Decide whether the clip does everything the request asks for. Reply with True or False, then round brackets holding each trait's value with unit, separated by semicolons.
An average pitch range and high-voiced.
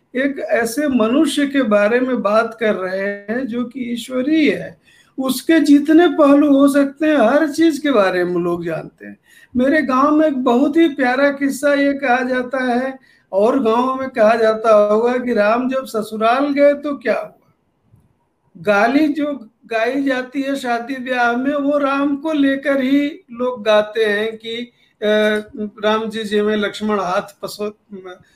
True (4.8 semitones; 250 Hz)